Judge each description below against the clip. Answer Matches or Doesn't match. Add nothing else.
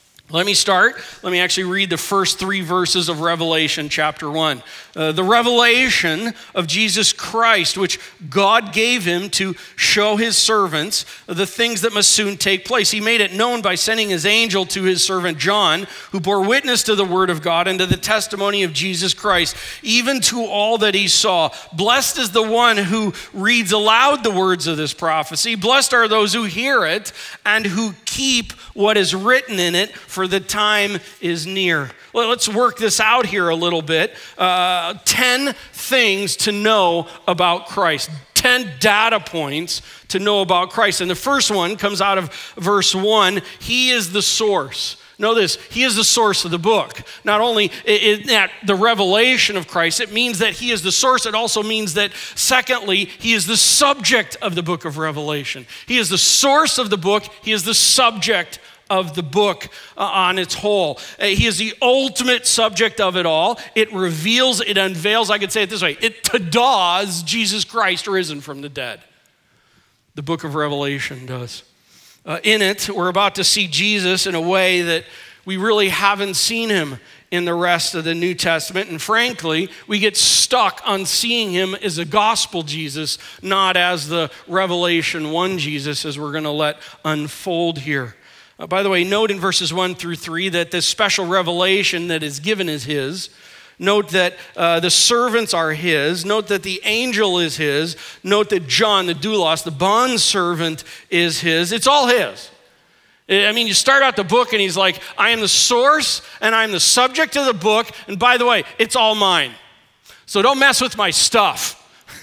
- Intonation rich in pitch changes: Doesn't match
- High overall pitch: Matches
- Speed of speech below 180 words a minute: Doesn't match